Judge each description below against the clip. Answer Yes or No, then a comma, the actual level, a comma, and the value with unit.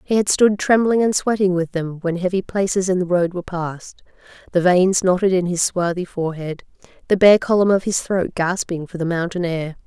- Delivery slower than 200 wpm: No, fast, 205 wpm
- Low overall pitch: No, medium, 180 Hz